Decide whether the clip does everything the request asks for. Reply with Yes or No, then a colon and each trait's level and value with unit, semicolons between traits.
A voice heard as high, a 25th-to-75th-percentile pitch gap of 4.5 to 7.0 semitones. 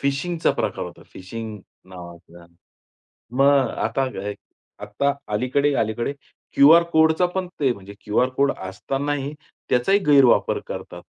No: low, 135 Hz; wide, 5.4 semitones